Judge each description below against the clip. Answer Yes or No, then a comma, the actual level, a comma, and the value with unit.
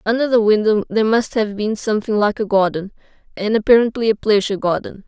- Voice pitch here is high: Yes, high, 215 Hz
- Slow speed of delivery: No, average, 190 wpm